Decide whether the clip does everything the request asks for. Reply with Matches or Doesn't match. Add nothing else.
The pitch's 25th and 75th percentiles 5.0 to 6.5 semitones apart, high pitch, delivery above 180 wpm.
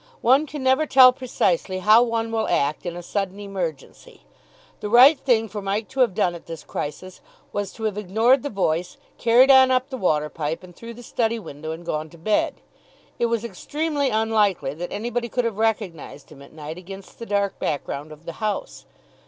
Matches